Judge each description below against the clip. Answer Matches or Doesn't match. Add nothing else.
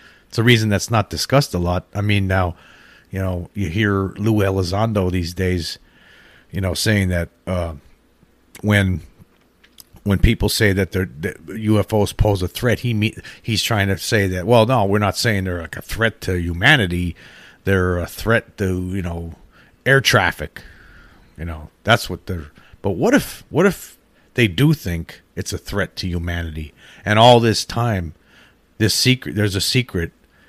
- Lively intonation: Doesn't match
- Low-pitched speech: Matches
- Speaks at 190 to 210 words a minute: Doesn't match